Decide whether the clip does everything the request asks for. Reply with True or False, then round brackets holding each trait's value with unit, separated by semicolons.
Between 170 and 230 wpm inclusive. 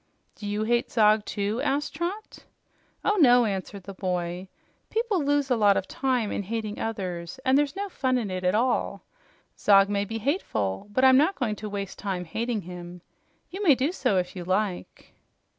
True (190 wpm)